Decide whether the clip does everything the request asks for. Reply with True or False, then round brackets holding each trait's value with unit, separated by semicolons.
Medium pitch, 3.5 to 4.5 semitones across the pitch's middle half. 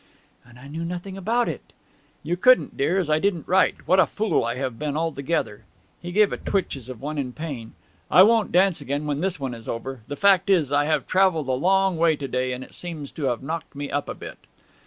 False (155 Hz; 5.5 semitones)